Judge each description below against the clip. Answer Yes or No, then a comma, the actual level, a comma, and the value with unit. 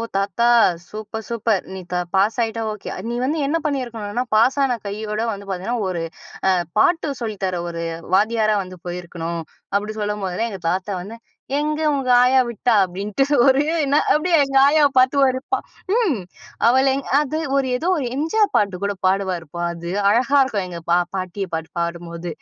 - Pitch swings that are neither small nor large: No, wide, 5.9 semitones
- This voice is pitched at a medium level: No, high, 215 Hz